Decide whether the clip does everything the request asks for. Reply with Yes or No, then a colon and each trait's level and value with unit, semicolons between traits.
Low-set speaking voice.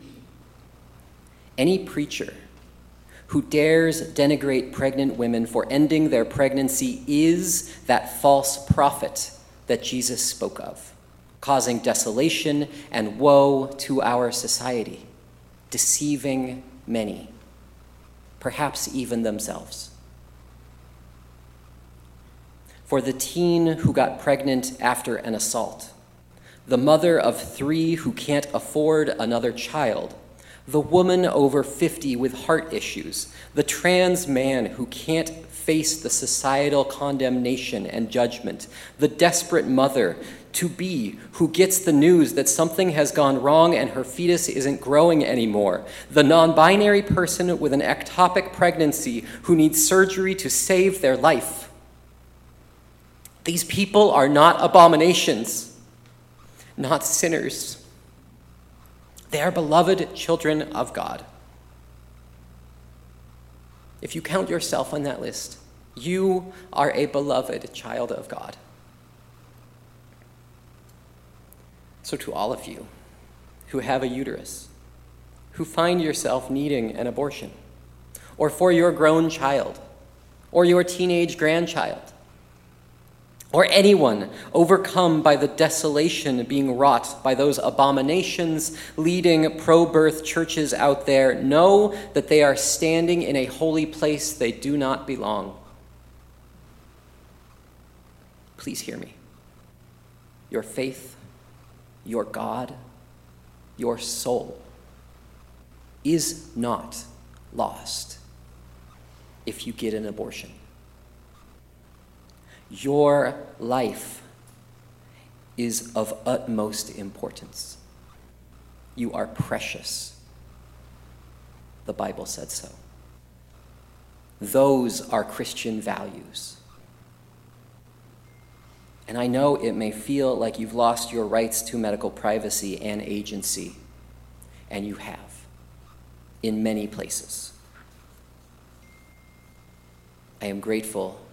Yes: low, 115 Hz